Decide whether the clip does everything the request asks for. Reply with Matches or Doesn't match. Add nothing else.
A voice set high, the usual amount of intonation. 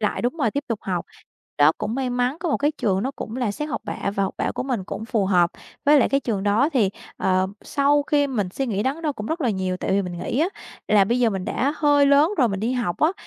Doesn't match